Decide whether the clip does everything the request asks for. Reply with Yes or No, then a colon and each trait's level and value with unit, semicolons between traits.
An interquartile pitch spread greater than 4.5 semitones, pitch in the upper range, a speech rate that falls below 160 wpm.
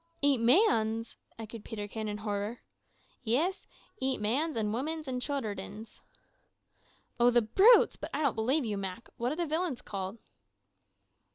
Yes: average, 4.9 semitones; high, 235 Hz; average, 145 wpm